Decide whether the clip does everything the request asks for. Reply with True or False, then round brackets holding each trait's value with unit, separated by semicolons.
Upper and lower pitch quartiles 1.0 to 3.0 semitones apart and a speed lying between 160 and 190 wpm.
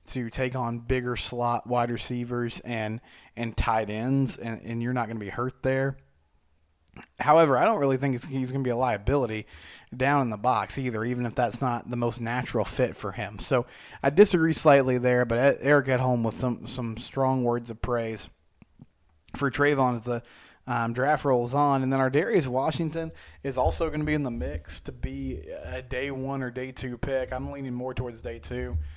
False (2.6 semitones; 205 wpm)